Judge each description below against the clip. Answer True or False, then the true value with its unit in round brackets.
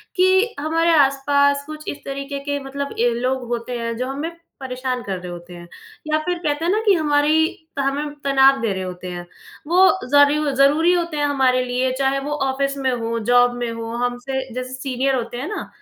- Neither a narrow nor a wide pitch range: True (3.1 semitones)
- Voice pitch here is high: True (275 Hz)